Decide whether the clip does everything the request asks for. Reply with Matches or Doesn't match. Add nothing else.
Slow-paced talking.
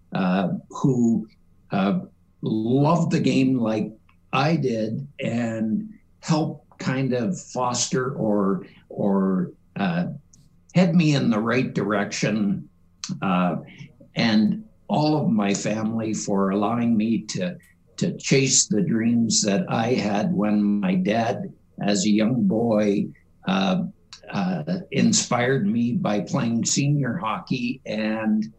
Matches